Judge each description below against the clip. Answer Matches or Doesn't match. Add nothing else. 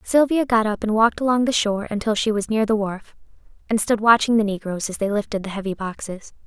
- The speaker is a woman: Matches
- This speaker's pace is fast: Matches